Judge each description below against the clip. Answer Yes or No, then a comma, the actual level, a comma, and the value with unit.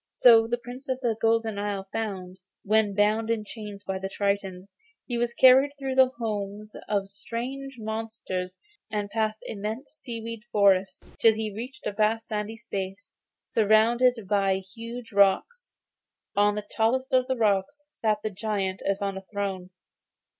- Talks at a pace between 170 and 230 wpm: No, average, 155 wpm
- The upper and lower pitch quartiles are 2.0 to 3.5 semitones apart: Yes, average, 2.8 semitones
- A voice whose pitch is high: Yes, high, 215 Hz